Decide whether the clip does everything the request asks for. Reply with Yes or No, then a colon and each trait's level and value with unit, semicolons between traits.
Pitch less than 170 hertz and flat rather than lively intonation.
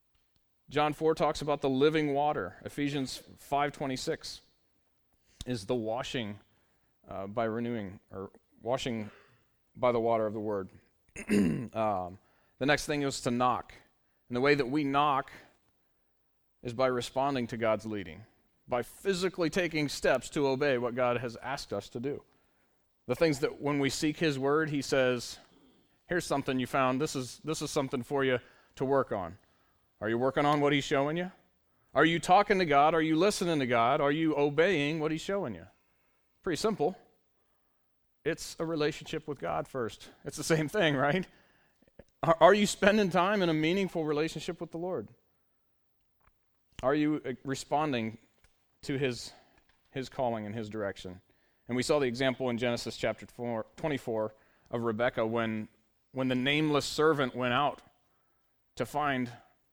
No: low, 135 Hz; average, 4.7 semitones